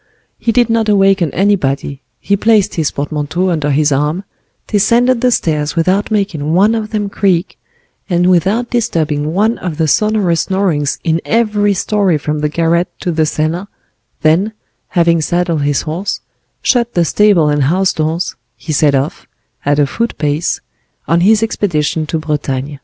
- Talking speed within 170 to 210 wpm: No, average, 160 wpm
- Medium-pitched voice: Yes, medium, 170 Hz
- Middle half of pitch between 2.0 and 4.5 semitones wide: No, average, 5.2 semitones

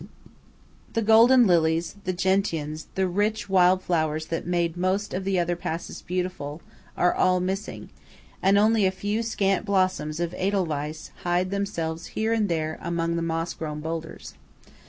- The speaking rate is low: No, average, 155 wpm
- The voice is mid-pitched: Yes, medium, 180 Hz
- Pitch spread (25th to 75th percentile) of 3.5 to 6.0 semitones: No, average, 3.1 semitones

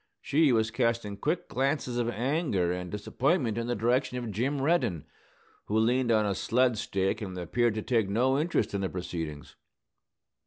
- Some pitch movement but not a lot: Yes, average, 4.5 semitones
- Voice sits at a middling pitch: No, low, 115 Hz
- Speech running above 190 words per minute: No, average, 170 wpm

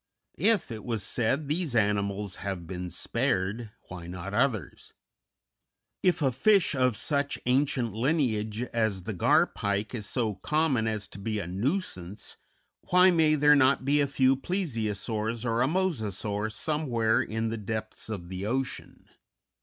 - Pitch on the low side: Yes, low, 115 Hz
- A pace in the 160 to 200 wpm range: No, average, 150 wpm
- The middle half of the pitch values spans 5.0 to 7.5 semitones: Yes, average, 5.3 semitones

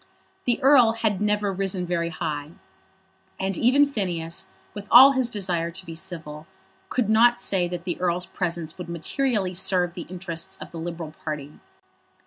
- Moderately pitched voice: Yes, medium, 180 Hz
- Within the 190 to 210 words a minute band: No, average, 160 wpm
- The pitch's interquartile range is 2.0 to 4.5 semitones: Yes, average, 3.9 semitones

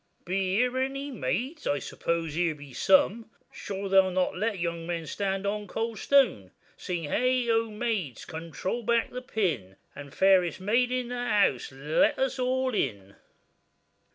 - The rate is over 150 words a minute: Yes, average, 175 wpm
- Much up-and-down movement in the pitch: Yes, wide, 6.3 semitones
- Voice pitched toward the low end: No, high, 195 Hz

